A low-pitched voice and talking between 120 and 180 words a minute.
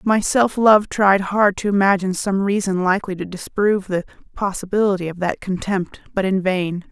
No: high, 195 Hz; average, 175 wpm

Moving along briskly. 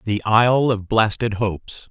No: average, 155 wpm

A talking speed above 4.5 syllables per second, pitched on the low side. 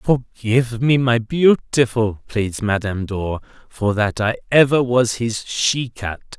No: 3.7 syllables/s; low, 115 Hz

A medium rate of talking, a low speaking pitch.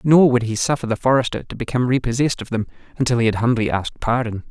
No: fast, 225 wpm; low, 120 Hz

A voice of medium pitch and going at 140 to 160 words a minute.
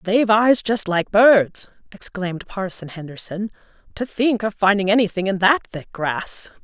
No: high, 200 Hz; average, 155 wpm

